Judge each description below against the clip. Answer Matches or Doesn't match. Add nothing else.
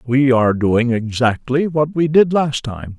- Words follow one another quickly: Doesn't match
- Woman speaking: Doesn't match